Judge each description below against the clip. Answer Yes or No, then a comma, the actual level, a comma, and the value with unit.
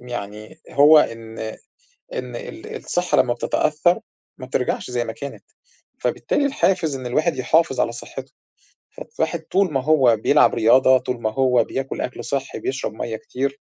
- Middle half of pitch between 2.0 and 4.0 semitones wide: No, average, 4.4 semitones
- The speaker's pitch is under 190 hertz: Yes, low, 135 Hz